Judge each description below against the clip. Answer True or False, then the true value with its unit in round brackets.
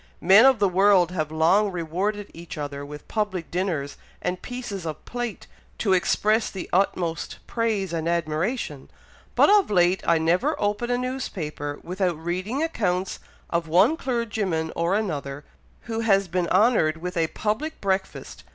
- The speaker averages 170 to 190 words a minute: False (150 wpm)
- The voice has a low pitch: False (185 Hz)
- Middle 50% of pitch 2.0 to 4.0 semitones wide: False (4.5 semitones)